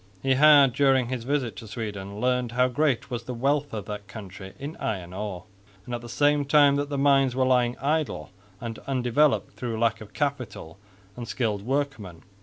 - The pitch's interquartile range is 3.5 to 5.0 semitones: Yes, average, 4.2 semitones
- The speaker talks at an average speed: Yes, average, 190 wpm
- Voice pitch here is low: Yes, low, 125 Hz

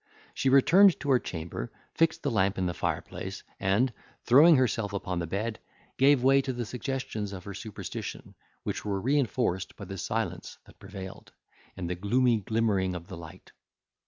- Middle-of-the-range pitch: No, low, 110 Hz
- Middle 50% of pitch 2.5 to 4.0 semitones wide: No, wide, 5.5 semitones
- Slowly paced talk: No, average, 170 wpm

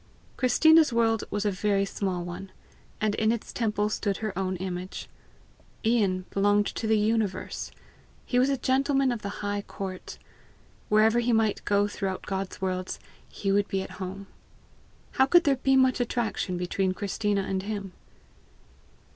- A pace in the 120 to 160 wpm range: Yes, average, 155 wpm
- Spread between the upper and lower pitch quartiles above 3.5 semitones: No, average, 3.2 semitones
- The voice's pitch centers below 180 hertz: No, high, 205 Hz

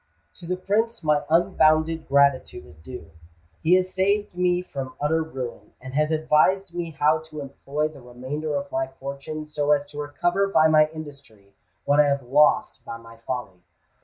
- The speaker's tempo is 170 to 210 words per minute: Yes, average, 175 wpm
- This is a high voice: No, medium, 150 Hz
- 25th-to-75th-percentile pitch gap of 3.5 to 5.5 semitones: No, average, 3.1 semitones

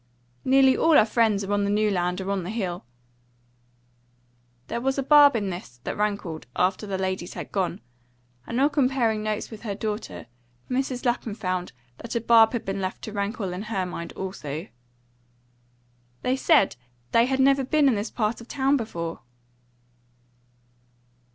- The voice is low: No, high, 215 Hz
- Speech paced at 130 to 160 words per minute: No, average, 170 wpm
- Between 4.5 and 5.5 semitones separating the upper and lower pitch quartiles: Yes, average, 4.8 semitones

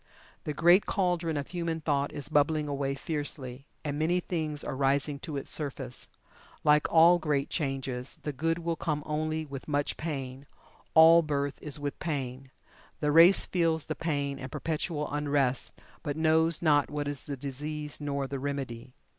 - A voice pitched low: No, medium, 150 Hz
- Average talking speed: Yes, average, 165 wpm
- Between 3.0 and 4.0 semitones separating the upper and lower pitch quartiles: No, narrow, 2.4 semitones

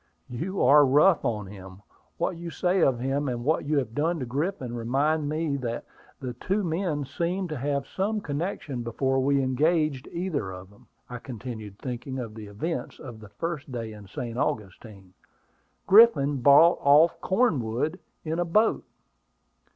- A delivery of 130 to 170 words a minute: Yes, average, 165 wpm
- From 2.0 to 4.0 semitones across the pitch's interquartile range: No, wide, 5.6 semitones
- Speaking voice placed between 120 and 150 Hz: Yes, medium, 140 Hz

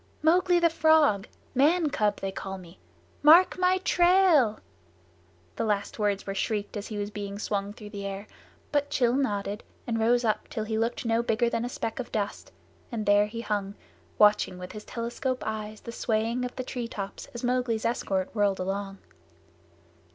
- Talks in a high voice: Yes, high, 220 Hz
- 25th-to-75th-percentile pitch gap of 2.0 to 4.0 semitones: Yes, average, 3.6 semitones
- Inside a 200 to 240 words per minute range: No, average, 175 wpm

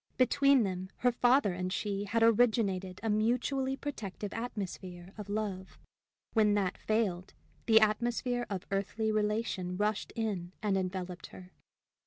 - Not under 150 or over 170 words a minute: No, slow, 135 wpm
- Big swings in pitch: No, average, 3.4 semitones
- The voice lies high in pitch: Yes, high, 210 Hz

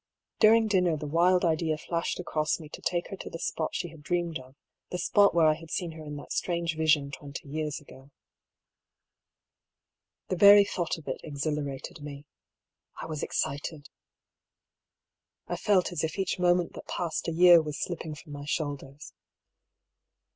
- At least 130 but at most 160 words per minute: No, average, 170 wpm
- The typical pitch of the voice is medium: Yes, medium, 160 Hz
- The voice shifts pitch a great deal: No, average, 3.0 semitones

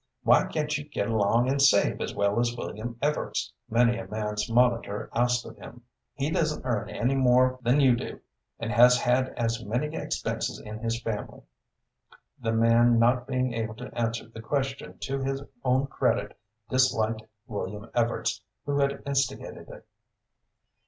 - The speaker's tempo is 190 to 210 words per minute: No, average, 160 wpm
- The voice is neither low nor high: No, low, 120 Hz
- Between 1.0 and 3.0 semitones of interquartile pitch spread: Yes, average, 2.7 semitones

